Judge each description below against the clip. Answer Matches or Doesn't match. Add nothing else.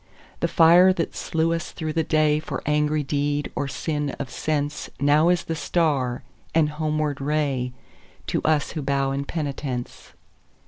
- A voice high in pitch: Doesn't match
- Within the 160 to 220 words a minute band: Doesn't match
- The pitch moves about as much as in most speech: Doesn't match